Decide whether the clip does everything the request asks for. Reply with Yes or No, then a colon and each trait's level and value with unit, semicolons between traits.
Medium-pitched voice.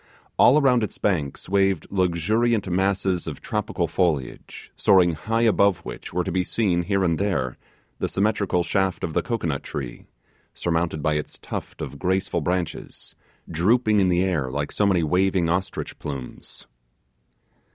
No: very low, 90 Hz